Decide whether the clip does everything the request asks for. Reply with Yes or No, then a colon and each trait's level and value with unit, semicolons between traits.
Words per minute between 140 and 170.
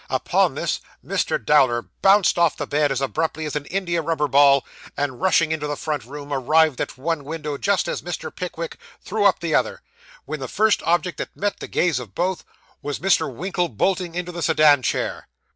No: average, 195 wpm